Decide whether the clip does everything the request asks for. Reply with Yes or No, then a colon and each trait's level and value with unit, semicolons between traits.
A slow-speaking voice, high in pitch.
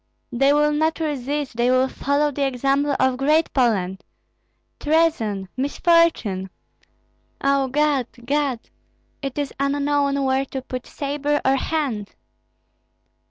Yes: slow, 115 wpm; very high, 275 Hz